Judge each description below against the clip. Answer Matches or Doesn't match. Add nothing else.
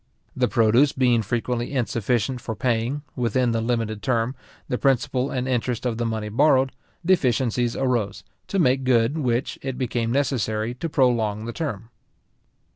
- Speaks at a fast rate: Doesn't match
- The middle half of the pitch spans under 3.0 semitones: Matches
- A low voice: Matches